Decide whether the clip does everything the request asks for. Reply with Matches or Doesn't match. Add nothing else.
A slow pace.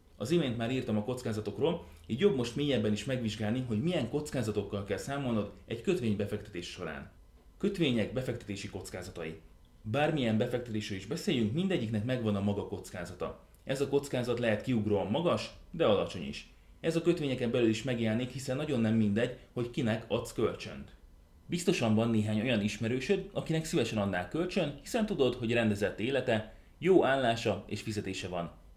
Doesn't match